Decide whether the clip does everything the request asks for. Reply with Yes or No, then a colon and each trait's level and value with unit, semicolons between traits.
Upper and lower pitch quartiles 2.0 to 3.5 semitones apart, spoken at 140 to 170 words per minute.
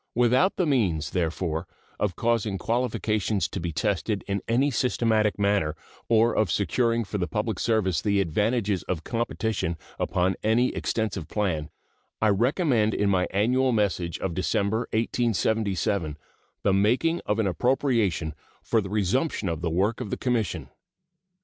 No: average, 3.9 semitones; average, 145 wpm